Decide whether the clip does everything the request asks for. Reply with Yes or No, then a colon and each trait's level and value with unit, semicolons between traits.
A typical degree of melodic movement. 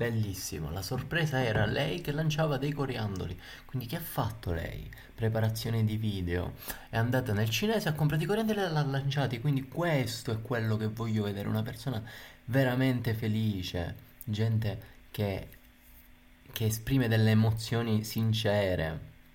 Yes: average, 3.9 semitones